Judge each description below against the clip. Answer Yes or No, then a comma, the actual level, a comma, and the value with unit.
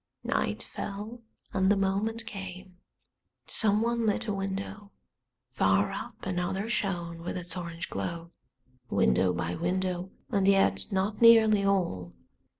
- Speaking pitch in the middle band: No, high, 195 Hz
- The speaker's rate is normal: No, slow, 125 wpm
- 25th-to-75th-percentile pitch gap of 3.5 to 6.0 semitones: No, average, 2.9 semitones